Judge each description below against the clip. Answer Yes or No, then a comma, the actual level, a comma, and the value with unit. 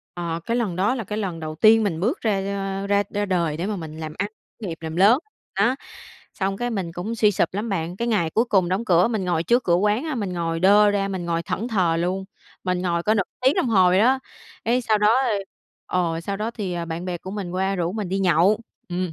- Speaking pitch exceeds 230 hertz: No, high, 190 Hz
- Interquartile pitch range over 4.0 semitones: No, average, 3.7 semitones